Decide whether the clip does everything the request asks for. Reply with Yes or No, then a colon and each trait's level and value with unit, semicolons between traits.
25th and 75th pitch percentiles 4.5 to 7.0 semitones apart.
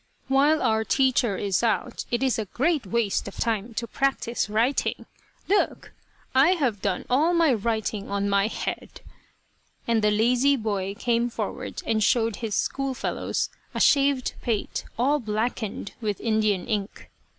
No: average, 4.0 semitones